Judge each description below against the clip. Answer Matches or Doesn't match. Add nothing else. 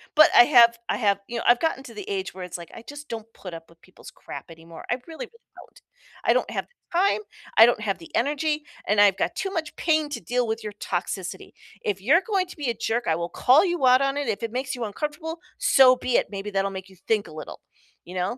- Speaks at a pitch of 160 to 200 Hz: Doesn't match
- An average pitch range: Doesn't match